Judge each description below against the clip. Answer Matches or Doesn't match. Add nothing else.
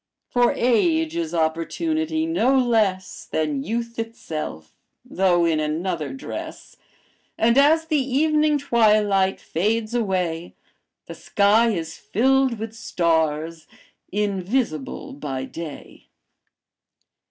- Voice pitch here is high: Matches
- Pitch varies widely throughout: Matches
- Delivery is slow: Matches